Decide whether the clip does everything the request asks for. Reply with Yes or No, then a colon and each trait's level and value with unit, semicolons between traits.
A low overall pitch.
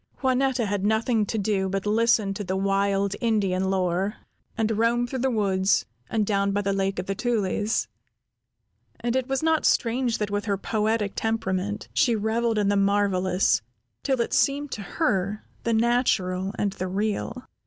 No: high, 210 Hz